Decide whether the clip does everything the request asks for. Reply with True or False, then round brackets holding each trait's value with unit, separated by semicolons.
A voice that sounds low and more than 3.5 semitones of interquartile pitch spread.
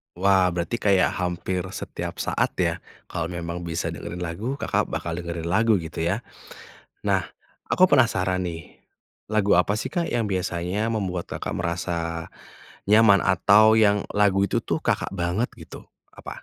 True (95 Hz; 3.9 semitones)